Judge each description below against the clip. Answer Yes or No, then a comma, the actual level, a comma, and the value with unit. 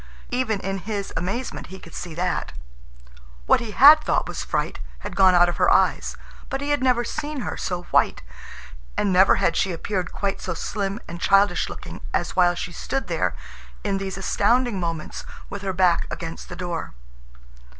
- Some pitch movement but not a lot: Yes, average, 3.9 semitones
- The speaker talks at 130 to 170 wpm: No, average, 180 wpm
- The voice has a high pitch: Yes, high, 195 Hz